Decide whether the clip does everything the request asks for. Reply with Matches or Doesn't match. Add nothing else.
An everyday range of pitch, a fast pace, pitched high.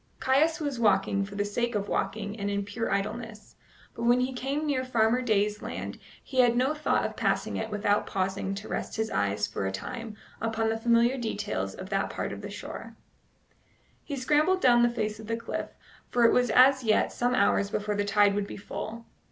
Matches